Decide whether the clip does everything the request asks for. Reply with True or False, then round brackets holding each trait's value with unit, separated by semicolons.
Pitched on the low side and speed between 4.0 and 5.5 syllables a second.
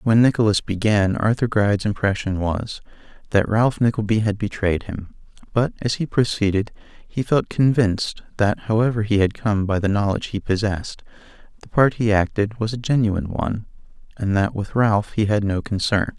True (105 Hz; 5.2 syllables/s)